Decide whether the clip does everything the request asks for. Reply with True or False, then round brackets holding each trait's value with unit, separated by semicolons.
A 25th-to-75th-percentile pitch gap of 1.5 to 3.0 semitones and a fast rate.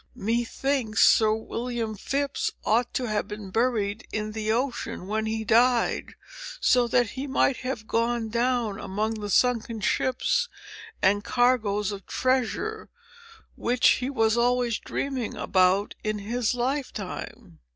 False (2.7 semitones; 135 wpm)